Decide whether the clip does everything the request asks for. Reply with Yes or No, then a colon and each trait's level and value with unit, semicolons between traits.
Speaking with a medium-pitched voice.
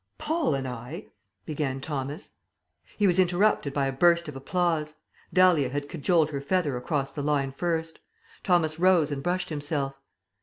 Yes: medium, 150 Hz